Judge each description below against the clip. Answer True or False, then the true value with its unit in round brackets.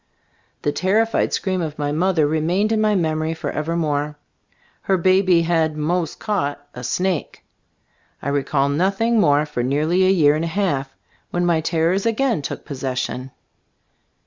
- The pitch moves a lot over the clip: False (4.3 semitones)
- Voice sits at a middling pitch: True (165 Hz)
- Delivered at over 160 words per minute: False (150 wpm)